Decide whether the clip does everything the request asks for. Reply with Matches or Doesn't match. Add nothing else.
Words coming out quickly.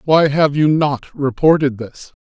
Doesn't match